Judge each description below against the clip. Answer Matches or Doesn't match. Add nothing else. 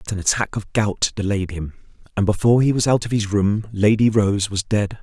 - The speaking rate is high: Matches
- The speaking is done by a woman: Doesn't match